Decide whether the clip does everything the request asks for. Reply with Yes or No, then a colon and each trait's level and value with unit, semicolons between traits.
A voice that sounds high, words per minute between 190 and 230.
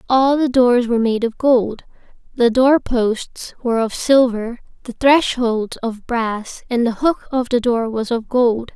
No: high, 240 Hz; average, 170 wpm